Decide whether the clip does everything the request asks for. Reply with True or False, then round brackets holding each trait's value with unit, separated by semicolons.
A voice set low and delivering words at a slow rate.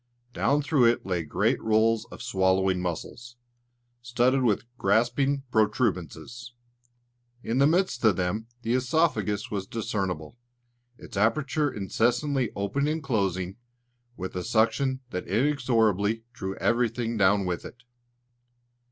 True (115 Hz; 120 wpm)